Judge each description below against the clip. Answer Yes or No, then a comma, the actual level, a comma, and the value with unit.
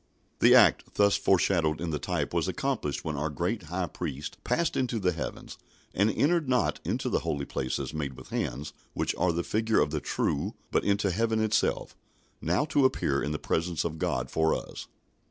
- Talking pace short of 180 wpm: No, average, 190 wpm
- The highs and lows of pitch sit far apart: Yes, wide, 6.3 semitones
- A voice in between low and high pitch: No, very low, 85 Hz